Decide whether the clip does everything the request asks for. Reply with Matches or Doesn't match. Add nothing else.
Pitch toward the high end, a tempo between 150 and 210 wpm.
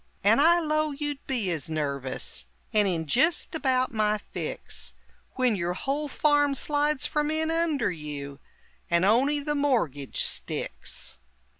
Doesn't match